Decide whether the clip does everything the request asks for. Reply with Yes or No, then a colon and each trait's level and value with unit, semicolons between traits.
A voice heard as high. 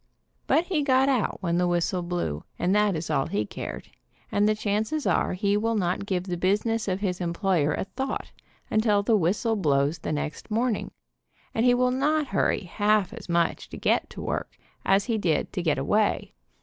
Yes: high, 200 Hz